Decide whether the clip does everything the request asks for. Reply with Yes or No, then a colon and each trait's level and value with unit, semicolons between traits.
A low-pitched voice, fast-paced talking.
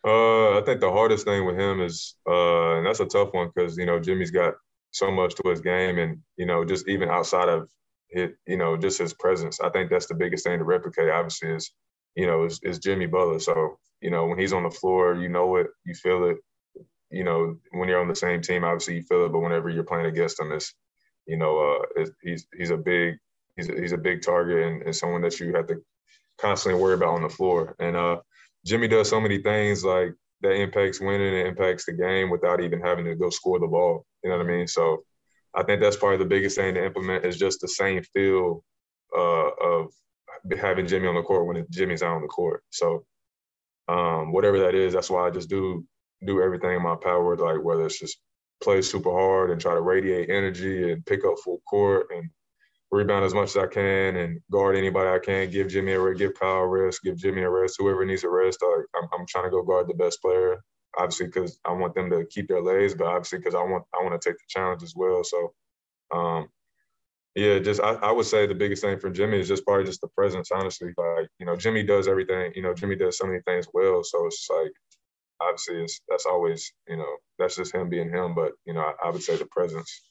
Yes: very low, 95 Hz; fast, 240 wpm